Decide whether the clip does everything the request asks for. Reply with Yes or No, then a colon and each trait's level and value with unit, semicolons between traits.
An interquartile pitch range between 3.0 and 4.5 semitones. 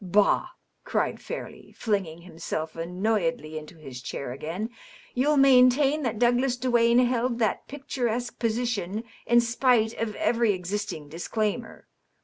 No: average, 5.3 semitones